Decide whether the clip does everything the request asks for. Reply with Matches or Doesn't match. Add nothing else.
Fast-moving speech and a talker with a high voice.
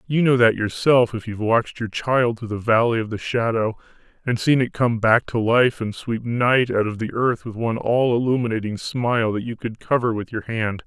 Doesn't match